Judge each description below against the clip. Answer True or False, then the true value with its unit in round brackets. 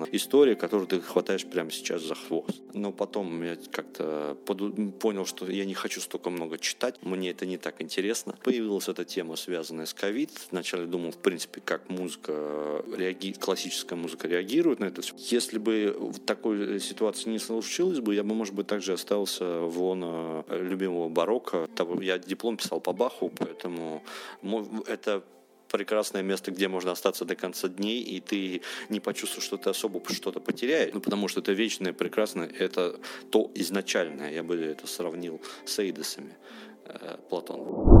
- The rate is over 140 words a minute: True (160 wpm)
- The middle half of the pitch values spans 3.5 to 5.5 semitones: False (3.1 semitones)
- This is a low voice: True (95 Hz)